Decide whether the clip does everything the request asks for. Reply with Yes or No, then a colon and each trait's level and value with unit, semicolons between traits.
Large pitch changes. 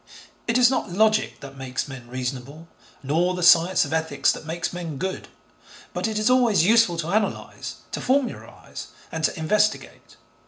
Yes: wide, 6.2 semitones